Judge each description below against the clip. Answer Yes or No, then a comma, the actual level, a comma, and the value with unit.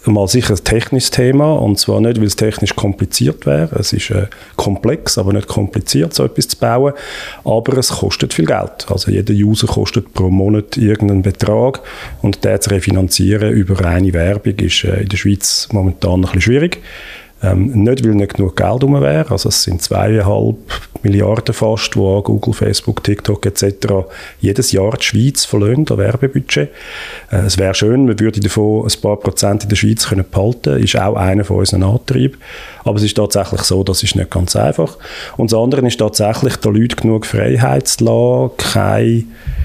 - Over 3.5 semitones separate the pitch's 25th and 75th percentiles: No, narrow, 2.6 semitones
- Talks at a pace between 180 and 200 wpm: Yes, average, 185 wpm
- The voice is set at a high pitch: No, low, 105 Hz